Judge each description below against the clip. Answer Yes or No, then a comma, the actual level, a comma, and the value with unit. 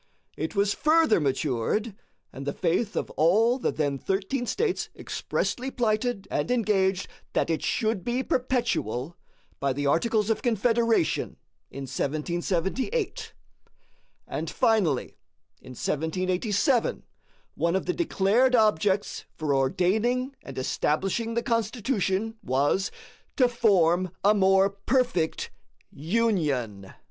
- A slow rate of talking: Yes, slow, 115 wpm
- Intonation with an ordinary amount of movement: No, wide, 6.6 semitones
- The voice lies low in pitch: No, high, 200 Hz